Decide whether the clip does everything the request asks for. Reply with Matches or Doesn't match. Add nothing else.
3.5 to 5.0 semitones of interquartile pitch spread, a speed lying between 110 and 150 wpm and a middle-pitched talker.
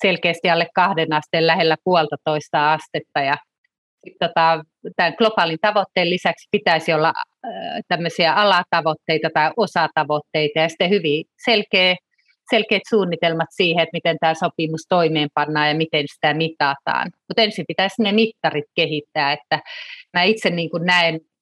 Matches